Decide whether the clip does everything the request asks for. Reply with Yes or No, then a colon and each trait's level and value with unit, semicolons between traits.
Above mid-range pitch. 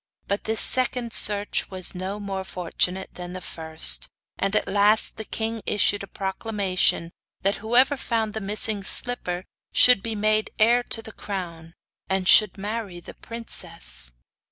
Yes: high, 205 Hz